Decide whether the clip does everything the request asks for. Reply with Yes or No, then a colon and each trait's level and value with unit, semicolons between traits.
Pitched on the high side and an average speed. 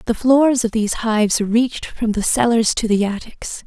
Yes: high, 225 Hz; average, 195 wpm